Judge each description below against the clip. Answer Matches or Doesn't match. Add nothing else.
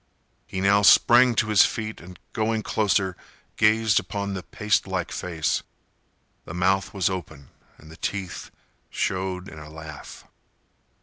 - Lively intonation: Doesn't match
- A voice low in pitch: Matches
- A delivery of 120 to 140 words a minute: Matches